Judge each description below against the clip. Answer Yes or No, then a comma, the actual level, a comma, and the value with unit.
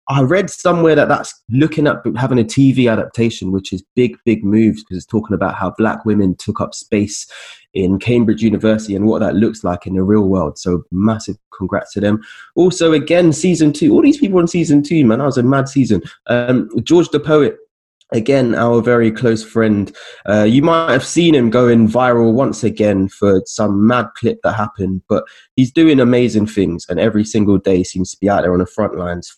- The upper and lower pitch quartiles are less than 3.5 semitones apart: No, average, 5.1 semitones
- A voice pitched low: Yes, low, 115 Hz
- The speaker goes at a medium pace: No, fast, 210 wpm